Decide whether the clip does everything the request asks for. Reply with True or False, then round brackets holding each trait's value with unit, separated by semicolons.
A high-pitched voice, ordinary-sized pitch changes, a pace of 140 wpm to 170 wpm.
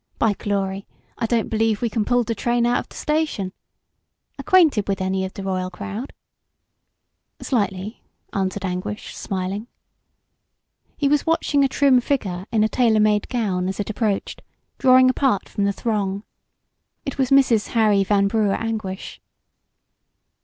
True (215 Hz; 3.7 semitones; 150 wpm)